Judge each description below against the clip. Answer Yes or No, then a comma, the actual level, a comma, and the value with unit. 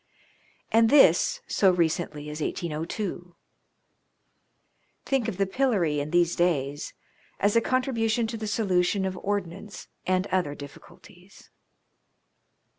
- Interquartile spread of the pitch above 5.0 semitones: No, average, 4.6 semitones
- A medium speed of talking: No, slow, 115 wpm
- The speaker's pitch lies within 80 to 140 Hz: No, medium, 185 Hz